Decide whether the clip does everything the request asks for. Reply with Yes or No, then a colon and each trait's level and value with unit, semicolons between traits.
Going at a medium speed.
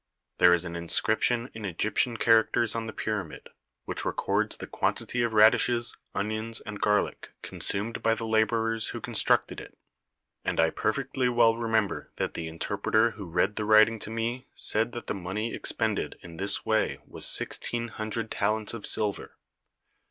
Yes: average, 165 wpm